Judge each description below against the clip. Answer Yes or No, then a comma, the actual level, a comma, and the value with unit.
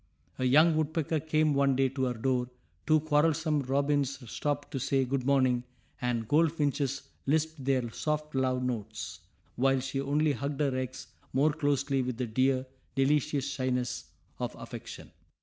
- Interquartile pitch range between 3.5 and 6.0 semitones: No, narrow, 2.5 semitones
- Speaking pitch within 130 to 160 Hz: Yes, low, 135 Hz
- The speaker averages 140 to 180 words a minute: Yes, average, 150 wpm